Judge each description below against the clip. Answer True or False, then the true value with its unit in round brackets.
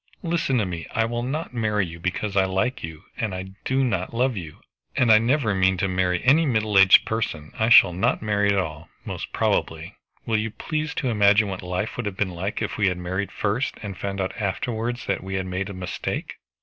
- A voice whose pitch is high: False (100 Hz)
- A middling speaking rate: False (225 wpm)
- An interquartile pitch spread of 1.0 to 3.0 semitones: False (3.7 semitones)